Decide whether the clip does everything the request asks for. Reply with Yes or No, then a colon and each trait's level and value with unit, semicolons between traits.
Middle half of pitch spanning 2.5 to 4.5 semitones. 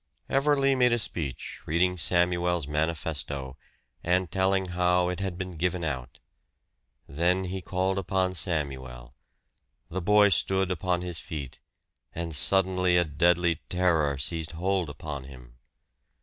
Yes: average, 3.4 semitones